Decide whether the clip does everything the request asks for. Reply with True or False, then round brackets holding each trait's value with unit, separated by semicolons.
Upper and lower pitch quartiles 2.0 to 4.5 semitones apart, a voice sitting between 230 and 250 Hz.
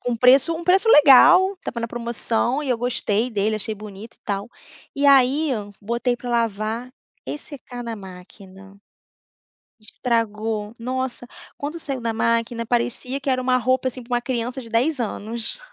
True (2.8 semitones; 240 Hz)